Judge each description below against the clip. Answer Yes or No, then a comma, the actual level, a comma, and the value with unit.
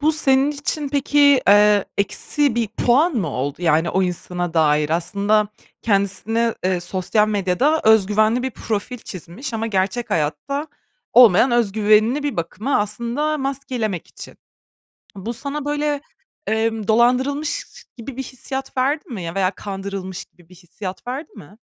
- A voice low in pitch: No, high, 220 Hz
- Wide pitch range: Yes, wide, 5.9 semitones